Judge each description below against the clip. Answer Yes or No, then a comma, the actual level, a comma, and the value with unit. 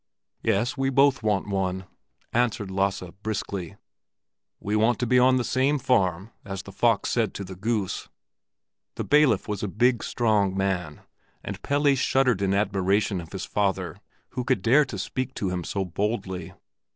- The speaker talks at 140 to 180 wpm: Yes, average, 165 wpm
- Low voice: Yes, low, 105 Hz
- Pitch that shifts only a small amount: No, average, 4.3 semitones